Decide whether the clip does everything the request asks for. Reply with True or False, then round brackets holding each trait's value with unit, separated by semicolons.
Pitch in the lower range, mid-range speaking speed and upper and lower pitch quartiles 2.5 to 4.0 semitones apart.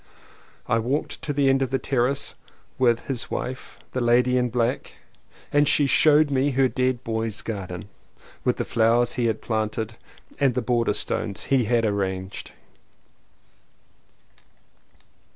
True (120 Hz; 150 wpm; 3.0 semitones)